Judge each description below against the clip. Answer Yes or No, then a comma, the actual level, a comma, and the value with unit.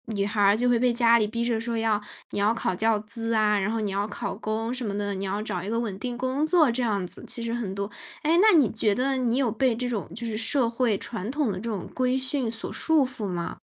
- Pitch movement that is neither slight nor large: Yes, average, 3.2 semitones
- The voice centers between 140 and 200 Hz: No, high, 230 Hz